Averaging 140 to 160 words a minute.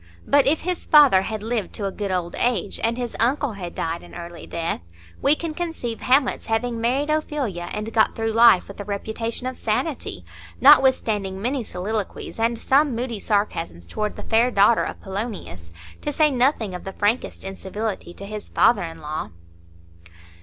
No: average, 175 wpm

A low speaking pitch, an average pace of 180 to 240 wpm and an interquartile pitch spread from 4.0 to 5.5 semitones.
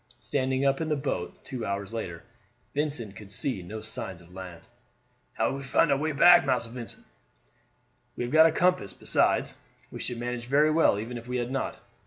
Yes: low, 125 Hz; average, 200 wpm; average, 4.9 semitones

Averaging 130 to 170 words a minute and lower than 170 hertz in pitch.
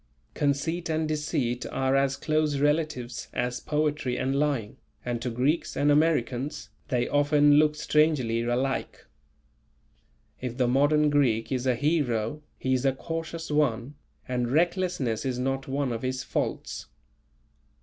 Yes: average, 140 wpm; low, 135 Hz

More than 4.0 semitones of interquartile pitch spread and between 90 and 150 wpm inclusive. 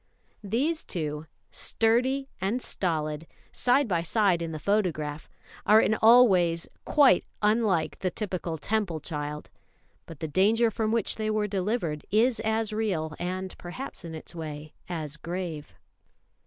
Yes: wide, 5.5 semitones; average, 140 wpm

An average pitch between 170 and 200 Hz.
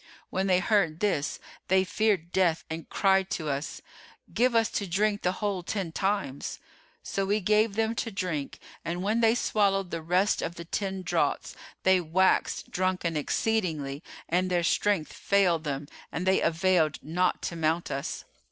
Yes: medium, 185 Hz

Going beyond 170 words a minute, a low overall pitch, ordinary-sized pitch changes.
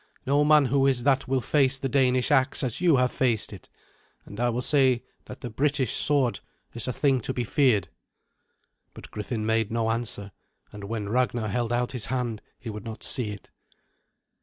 Yes: average, 190 wpm; low, 125 Hz; average, 3.1 semitones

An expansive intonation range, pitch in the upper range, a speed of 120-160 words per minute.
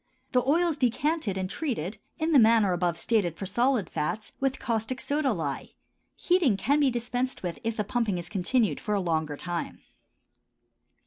No: wide, 6.4 semitones; high, 225 Hz; average, 175 wpm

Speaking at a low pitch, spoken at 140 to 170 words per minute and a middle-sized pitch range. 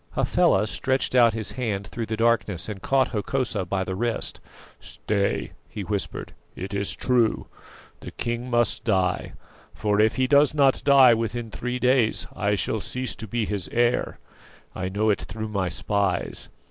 Yes: low, 110 Hz; average, 165 wpm; average, 3.4 semitones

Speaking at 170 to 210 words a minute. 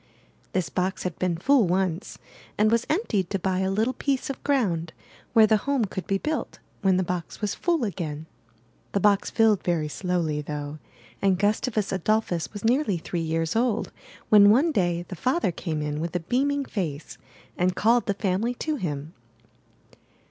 Yes: average, 175 wpm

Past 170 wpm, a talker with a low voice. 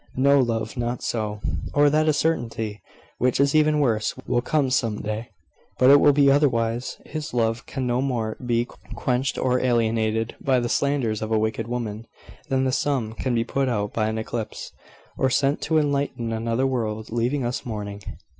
Yes: average, 185 wpm; low, 120 Hz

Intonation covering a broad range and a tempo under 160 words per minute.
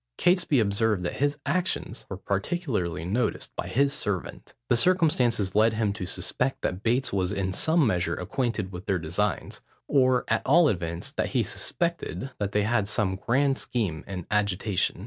No: wide, 6.0 semitones; average, 165 wpm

